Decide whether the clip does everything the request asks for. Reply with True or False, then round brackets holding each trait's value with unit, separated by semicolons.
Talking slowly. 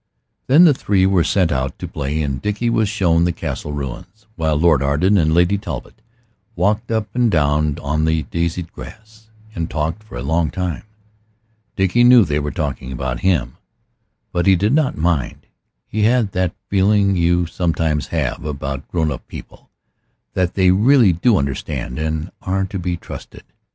False (170 wpm)